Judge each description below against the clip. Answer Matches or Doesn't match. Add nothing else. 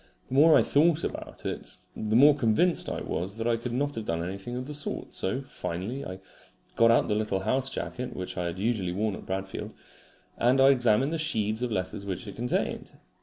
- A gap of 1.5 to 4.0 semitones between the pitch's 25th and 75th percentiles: Doesn't match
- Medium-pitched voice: Doesn't match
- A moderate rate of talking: Doesn't match